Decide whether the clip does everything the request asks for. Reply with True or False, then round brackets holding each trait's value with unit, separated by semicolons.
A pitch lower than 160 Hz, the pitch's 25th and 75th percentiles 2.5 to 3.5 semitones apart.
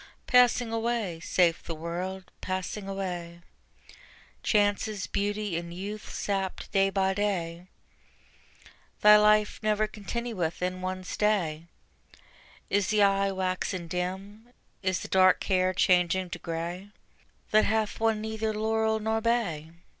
False (195 Hz; 2.9 semitones)